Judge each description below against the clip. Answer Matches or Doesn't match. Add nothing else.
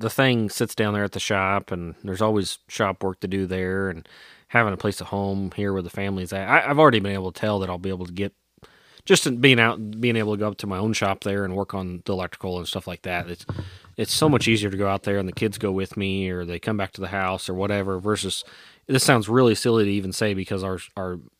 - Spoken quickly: Matches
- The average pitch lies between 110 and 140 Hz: Doesn't match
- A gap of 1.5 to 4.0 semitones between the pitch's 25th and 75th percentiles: Matches